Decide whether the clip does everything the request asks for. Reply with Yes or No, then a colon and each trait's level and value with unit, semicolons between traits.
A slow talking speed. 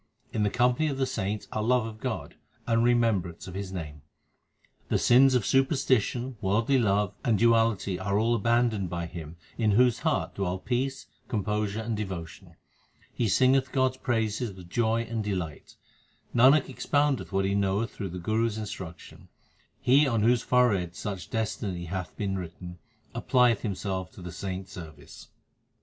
No: average, 165 wpm